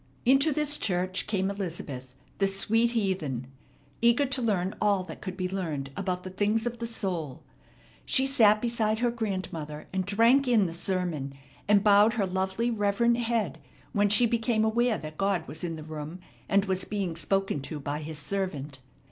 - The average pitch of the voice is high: Yes, high, 195 Hz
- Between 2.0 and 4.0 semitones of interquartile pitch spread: No, average, 4.8 semitones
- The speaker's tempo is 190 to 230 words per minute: No, average, 175 wpm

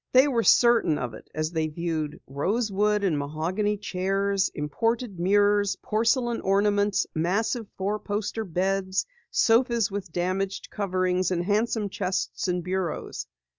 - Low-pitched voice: No, high, 195 Hz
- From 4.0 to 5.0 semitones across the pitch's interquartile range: No, average, 2.9 semitones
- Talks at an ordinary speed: No, slow, 130 wpm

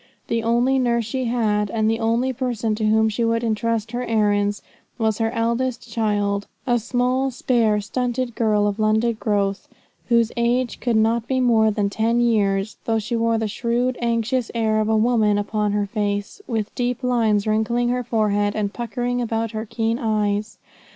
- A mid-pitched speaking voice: No, high, 225 Hz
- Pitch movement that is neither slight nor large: No, narrow, 2.0 semitones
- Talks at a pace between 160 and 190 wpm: Yes, average, 175 wpm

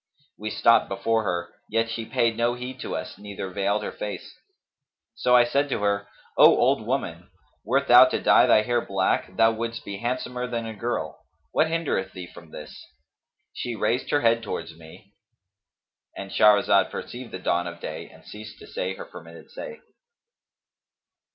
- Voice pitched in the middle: No, low, 115 Hz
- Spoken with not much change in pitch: No, average, 3.8 semitones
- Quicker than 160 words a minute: Yes, average, 170 wpm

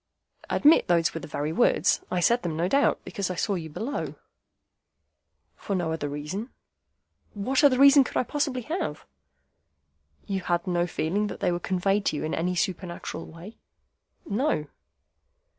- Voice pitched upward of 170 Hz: Yes, medium, 185 Hz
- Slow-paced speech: No, average, 160 wpm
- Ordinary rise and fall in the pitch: No, wide, 6.1 semitones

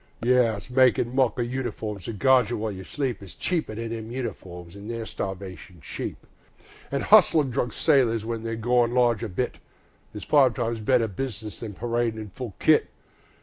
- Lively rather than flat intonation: No, average, 2.9 semitones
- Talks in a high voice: No, low, 115 Hz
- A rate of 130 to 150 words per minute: No, average, 180 wpm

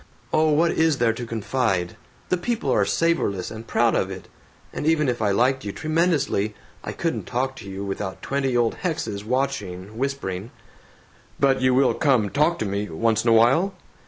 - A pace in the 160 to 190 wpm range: Yes, average, 185 wpm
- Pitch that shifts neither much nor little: No, wide, 5.7 semitones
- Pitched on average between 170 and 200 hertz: No, low, 120 Hz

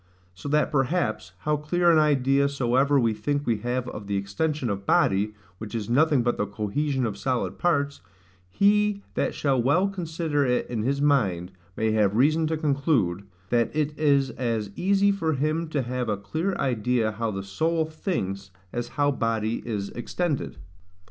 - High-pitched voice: No, low, 135 Hz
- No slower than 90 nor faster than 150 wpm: No, average, 175 wpm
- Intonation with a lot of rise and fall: Yes, wide, 5.9 semitones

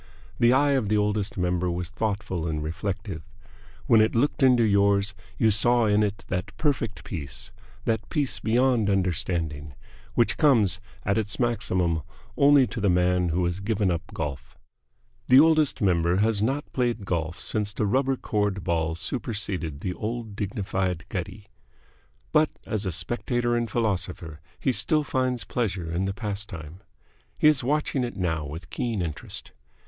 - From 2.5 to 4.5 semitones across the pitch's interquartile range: No, average, 5.1 semitones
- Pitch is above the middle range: No, low, 100 Hz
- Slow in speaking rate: No, average, 155 wpm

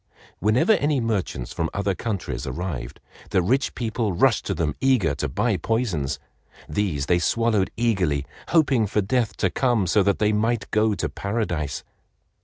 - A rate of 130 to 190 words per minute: Yes, average, 160 wpm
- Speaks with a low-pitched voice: Yes, low, 105 Hz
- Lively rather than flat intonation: No, average, 5.0 semitones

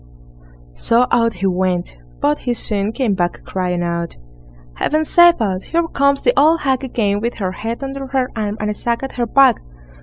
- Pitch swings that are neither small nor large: No, wide, 6.0 semitones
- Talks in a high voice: Yes, high, 230 Hz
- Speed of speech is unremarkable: Yes, average, 190 wpm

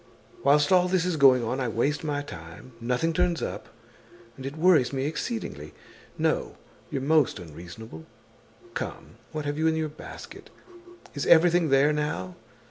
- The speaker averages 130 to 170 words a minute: Yes, average, 155 wpm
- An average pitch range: Yes, average, 4.2 semitones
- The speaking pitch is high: No, medium, 145 Hz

